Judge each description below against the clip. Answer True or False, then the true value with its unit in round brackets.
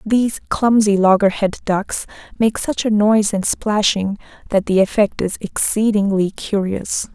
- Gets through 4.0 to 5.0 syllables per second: True (4.5 syllables/s)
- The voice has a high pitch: True (205 Hz)